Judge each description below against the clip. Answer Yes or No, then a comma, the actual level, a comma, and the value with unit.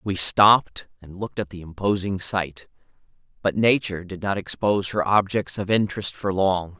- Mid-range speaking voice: No, very low, 95 Hz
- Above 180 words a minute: No, average, 170 wpm